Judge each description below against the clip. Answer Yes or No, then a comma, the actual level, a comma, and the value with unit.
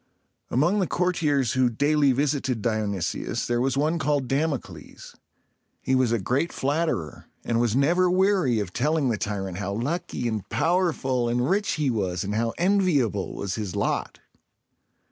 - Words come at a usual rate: Yes, average, 160 wpm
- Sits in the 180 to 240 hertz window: No, low, 130 Hz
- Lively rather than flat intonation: Yes, wide, 6.0 semitones